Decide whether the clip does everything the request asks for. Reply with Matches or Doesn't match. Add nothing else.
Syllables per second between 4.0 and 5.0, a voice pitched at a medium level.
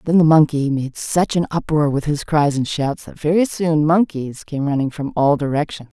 Matches